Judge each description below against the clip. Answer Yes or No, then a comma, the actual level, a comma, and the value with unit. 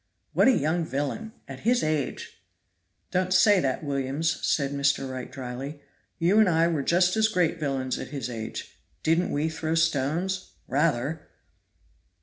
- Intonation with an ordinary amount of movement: Yes, average, 4.5 semitones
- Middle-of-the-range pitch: Yes, medium, 155 Hz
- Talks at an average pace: Yes, average, 155 wpm